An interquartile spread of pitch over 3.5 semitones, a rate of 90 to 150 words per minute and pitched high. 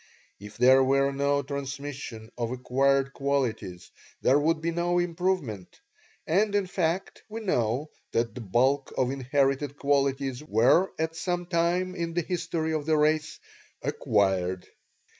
No: average, 4.7 semitones; average, 140 wpm; medium, 140 Hz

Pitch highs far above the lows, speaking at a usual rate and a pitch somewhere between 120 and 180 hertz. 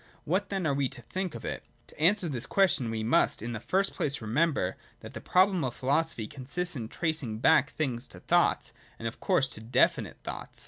No: wide, 7.0 semitones; fast, 215 wpm; medium, 140 Hz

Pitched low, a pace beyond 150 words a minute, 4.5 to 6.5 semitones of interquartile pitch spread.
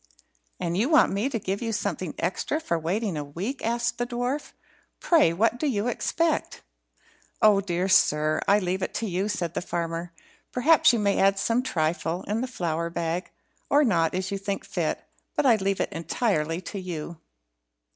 No: high, 195 Hz; average, 185 wpm; wide, 5.6 semitones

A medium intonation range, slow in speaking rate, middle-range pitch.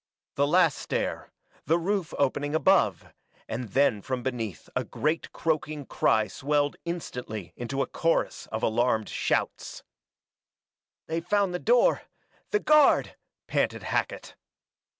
No: wide, 5.7 semitones; slow, 125 wpm; medium, 145 Hz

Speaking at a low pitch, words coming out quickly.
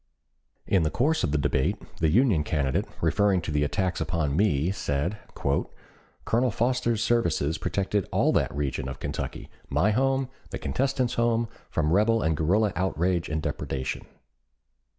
No: very low, 95 Hz; average, 150 wpm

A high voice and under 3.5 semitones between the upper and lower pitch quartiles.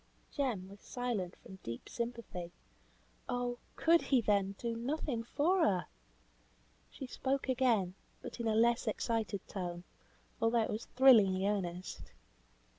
No: high, 230 Hz; average, 4.4 semitones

